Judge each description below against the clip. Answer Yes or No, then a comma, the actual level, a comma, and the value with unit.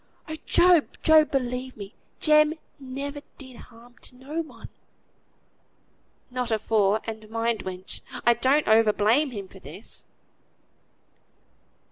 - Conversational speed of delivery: No, slow, 120 wpm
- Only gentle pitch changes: No, average, 4.5 semitones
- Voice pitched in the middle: No, very high, 250 Hz